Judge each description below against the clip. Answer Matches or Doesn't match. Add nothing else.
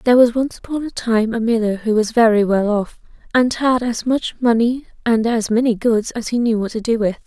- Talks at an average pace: Doesn't match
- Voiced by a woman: Matches